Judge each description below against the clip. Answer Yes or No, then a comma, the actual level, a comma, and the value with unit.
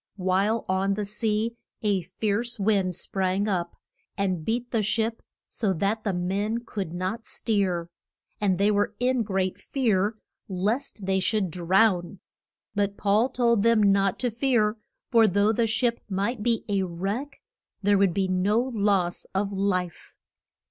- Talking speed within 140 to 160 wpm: Yes, average, 150 wpm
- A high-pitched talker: Yes, high, 205 Hz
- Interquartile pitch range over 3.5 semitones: No, average, 2.9 semitones